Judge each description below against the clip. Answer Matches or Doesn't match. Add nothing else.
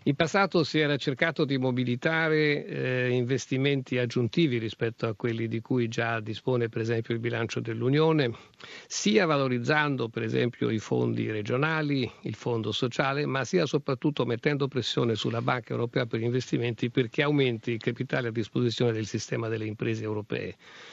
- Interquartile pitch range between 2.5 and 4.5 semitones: Matches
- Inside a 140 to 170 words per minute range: Matches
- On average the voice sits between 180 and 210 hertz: Doesn't match